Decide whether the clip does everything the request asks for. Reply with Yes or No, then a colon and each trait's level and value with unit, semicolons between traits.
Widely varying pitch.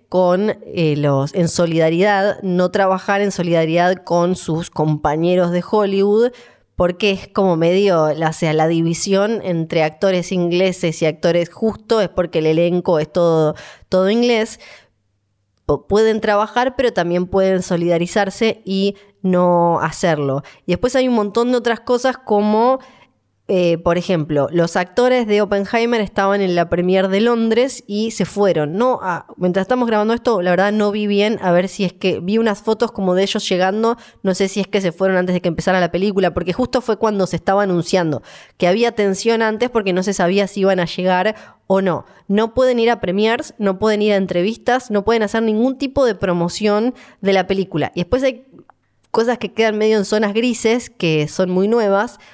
No: average, 3.8 semitones